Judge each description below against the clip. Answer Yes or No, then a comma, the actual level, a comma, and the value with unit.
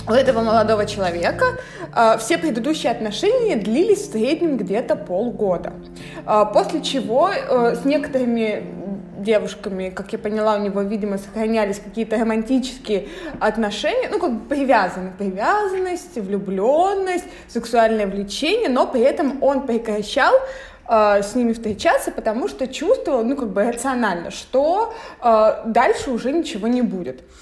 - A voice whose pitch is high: Yes, high, 230 Hz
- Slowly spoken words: No, average, 135 wpm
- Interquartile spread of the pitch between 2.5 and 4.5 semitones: No, wide, 5.4 semitones